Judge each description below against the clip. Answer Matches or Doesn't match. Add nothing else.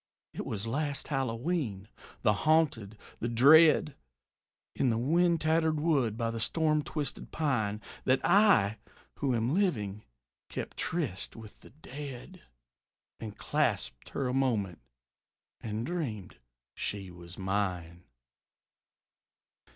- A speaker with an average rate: Doesn't match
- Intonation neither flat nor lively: Doesn't match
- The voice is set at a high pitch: Doesn't match